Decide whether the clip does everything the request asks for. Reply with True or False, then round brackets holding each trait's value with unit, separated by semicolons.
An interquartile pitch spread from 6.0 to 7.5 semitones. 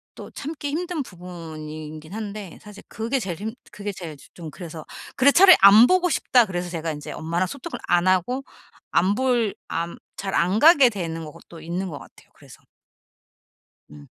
True (6.7 semitones)